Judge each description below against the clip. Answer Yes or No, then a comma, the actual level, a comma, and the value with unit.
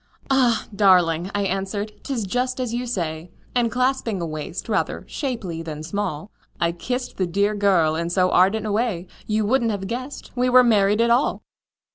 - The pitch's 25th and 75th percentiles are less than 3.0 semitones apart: No, average, 5.2 semitones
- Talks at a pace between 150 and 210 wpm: Yes, average, 180 wpm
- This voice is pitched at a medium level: No, high, 205 Hz